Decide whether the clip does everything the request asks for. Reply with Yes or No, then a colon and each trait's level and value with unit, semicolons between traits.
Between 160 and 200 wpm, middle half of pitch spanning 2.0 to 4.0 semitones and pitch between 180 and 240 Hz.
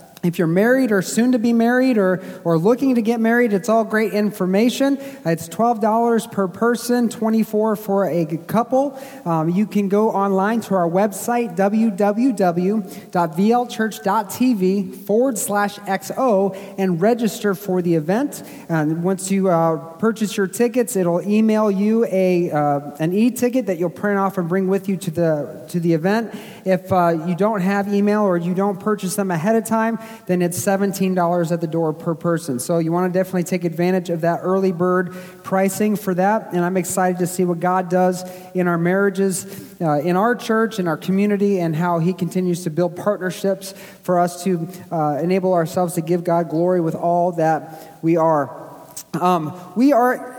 Yes: average, 175 wpm; average, 3.5 semitones; high, 190 Hz